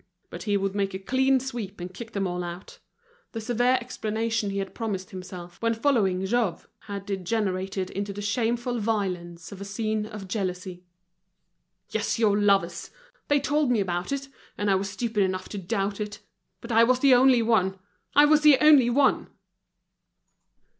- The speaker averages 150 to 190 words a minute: Yes, average, 175 wpm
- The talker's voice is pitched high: Yes, high, 205 Hz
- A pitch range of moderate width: Yes, average, 3.8 semitones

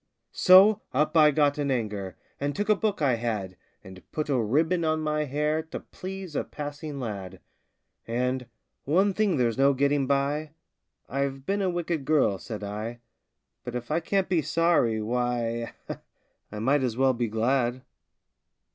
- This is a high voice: No, medium, 140 Hz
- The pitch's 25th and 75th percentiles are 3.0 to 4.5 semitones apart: No, average, 4.9 semitones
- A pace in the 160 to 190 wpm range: Yes, average, 165 wpm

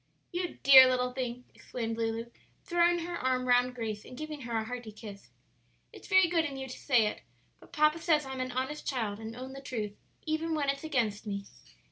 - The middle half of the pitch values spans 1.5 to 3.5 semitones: No, average, 5.0 semitones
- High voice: Yes, very high, 255 Hz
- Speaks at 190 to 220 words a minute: Yes, fast, 205 wpm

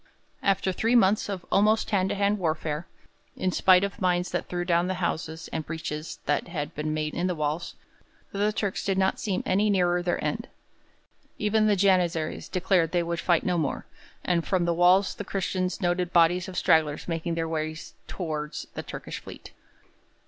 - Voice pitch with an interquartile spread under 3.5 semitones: Yes, average, 2.7 semitones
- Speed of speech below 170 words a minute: No, average, 185 wpm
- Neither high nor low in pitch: Yes, medium, 180 Hz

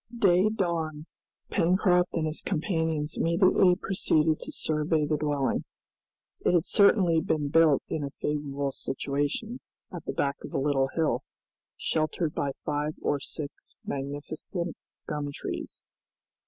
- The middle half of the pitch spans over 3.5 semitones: No, average, 3.2 semitones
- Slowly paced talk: Yes, slow, 130 wpm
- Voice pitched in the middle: Yes, medium, 155 Hz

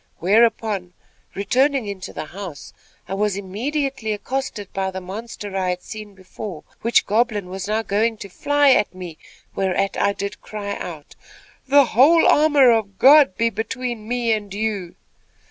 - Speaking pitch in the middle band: No, high, 210 Hz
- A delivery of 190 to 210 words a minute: No, average, 155 wpm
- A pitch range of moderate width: Yes, average, 3.7 semitones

